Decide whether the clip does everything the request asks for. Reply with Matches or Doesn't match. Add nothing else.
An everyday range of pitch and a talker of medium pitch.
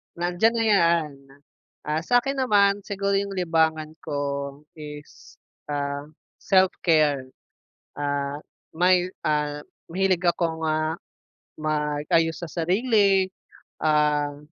Matches